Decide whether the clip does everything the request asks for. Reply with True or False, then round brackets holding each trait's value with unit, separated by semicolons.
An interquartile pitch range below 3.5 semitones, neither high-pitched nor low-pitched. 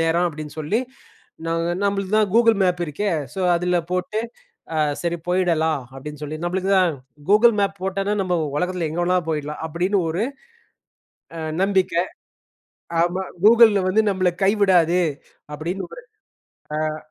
True (3.0 semitones; 180 Hz)